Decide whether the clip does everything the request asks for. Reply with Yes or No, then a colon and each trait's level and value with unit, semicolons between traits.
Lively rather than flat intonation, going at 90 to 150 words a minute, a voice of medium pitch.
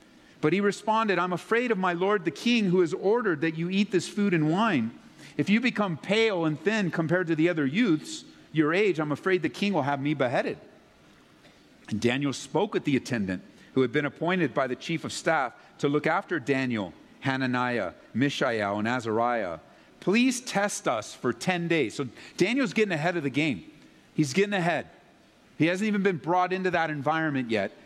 No: wide, 5.9 semitones; average, 190 wpm; medium, 170 Hz